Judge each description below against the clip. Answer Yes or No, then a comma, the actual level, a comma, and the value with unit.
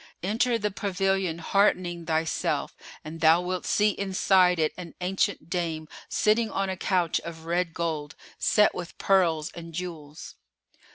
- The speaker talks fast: No, average, 145 wpm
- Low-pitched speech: No, medium, 180 Hz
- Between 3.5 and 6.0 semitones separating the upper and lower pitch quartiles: No, average, 2.8 semitones